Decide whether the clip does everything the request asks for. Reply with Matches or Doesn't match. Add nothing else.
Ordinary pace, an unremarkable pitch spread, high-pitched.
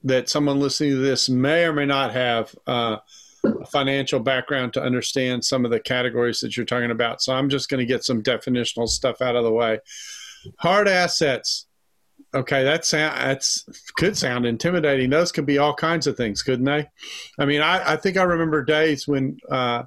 Doesn't match